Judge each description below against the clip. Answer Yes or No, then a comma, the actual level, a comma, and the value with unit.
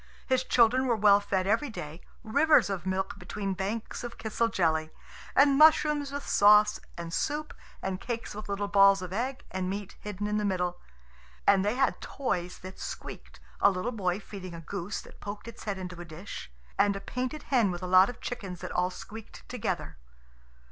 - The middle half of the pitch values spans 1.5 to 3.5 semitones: No, average, 4.0 semitones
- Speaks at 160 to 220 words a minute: Yes, average, 190 wpm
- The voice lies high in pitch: Yes, high, 205 Hz